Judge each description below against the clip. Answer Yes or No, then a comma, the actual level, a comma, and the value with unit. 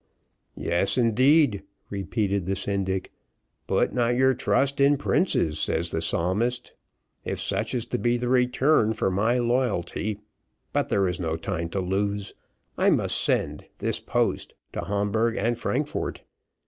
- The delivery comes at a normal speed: Yes, average, 145 wpm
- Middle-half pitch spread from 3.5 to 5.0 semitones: Yes, average, 4.4 semitones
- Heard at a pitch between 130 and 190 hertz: No, low, 110 Hz